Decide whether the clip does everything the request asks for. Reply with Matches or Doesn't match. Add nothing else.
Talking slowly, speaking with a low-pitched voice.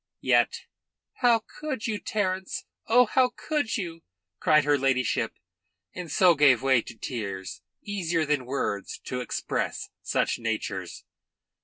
Doesn't match